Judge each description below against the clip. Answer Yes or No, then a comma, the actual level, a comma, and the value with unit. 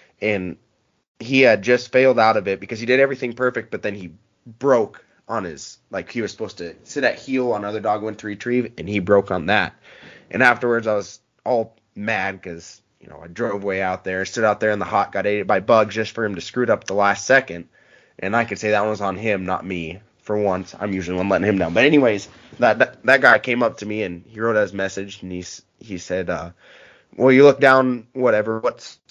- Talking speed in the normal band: No, fast, 235 wpm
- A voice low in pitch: Yes, low, 105 Hz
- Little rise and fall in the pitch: No, average, 3.3 semitones